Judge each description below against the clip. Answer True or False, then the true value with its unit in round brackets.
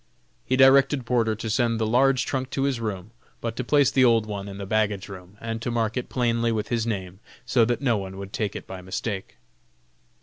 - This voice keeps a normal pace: False (225 wpm)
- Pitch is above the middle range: False (115 Hz)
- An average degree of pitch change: True (3.6 semitones)